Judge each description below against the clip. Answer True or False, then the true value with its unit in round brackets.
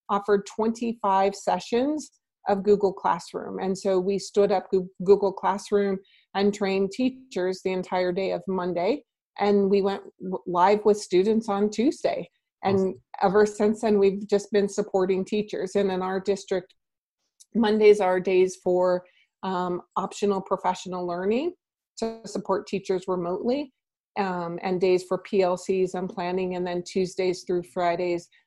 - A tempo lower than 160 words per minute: True (140 wpm)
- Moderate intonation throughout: False (1.8 semitones)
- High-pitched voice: True (195 Hz)